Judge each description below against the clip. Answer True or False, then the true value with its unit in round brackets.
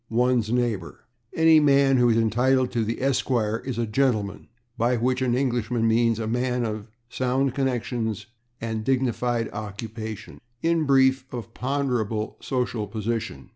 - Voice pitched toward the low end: True (120 Hz)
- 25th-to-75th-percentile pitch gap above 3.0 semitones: False (2.7 semitones)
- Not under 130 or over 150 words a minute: True (140 wpm)